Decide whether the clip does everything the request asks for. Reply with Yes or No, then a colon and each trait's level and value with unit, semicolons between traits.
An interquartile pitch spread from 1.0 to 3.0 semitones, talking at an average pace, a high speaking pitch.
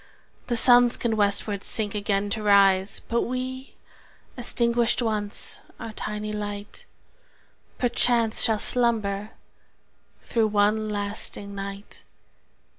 No: narrow, 2.5 semitones; slow, 110 wpm; high, 215 Hz